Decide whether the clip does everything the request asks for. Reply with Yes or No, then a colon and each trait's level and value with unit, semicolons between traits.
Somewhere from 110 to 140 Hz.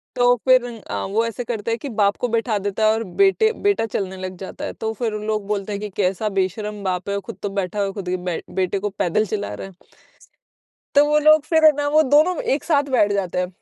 No: high, 210 Hz